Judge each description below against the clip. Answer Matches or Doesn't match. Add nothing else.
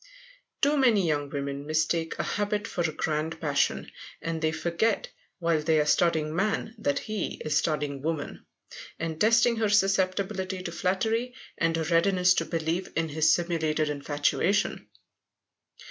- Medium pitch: Matches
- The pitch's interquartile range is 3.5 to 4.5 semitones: Matches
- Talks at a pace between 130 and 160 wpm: Matches